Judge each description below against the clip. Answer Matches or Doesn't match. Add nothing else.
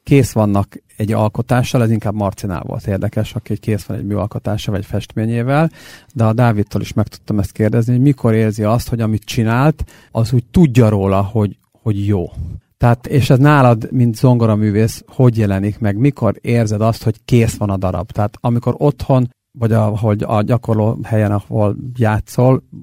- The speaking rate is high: Matches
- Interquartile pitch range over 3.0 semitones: Doesn't match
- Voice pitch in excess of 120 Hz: Doesn't match